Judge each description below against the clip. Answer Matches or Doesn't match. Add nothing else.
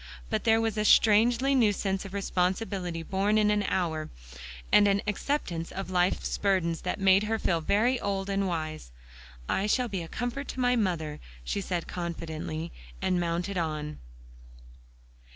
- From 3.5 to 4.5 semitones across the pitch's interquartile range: Matches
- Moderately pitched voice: Doesn't match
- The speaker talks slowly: Doesn't match